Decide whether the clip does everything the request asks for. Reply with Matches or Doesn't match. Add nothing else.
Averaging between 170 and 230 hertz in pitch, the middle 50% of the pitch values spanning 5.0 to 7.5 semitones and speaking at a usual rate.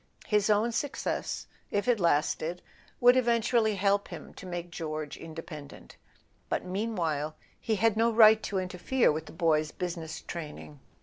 Matches